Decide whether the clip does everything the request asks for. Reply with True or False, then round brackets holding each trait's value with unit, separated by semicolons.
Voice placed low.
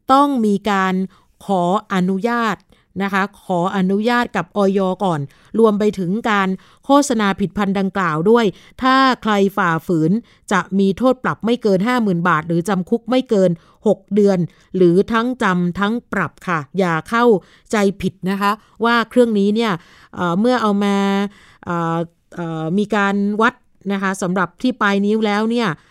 False (200 Hz)